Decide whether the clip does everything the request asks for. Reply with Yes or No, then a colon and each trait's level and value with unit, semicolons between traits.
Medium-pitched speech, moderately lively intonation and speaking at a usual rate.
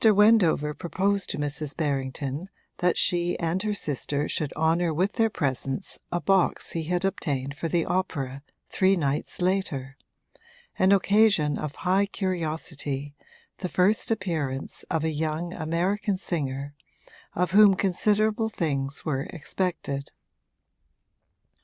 No: medium, 170 Hz; average, 4.7 semitones; slow, 125 wpm